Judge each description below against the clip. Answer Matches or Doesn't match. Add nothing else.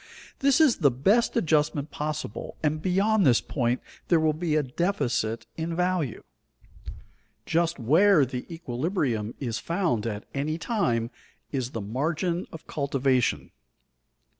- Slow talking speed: Matches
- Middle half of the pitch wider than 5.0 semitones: Matches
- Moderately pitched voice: Matches